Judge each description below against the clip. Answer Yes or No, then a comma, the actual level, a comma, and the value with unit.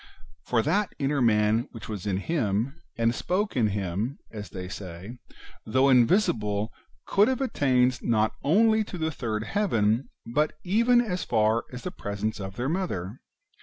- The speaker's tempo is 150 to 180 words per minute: Yes, average, 160 wpm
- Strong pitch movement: Yes, wide, 7.1 semitones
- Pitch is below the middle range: Yes, low, 120 Hz